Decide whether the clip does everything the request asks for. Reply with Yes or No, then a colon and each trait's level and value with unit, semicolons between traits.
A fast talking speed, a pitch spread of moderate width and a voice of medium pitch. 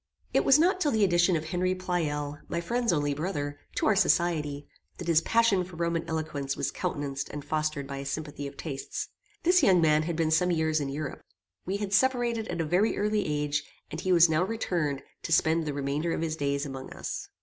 Yes: fast, 215 wpm; average, 3.9 semitones; medium, 160 Hz